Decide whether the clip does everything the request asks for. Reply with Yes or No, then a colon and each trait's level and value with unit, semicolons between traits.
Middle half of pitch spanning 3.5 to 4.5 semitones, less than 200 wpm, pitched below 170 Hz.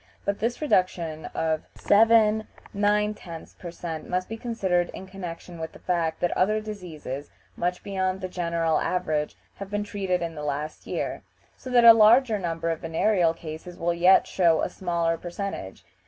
No: average, 3.8 semitones; average, 170 wpm; medium, 180 Hz